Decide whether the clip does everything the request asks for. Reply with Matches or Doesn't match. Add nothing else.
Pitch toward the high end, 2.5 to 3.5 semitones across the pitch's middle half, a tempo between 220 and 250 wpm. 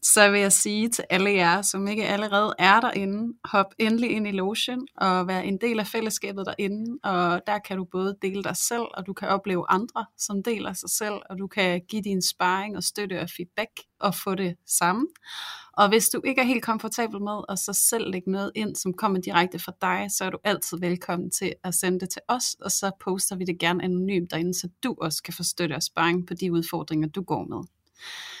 Matches